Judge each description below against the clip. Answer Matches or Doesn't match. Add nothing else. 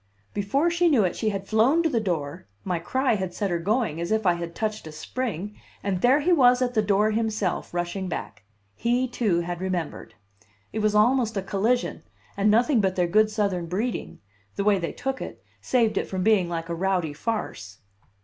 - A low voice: Doesn't match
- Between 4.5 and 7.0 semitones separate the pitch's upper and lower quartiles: Matches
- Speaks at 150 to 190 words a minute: Doesn't match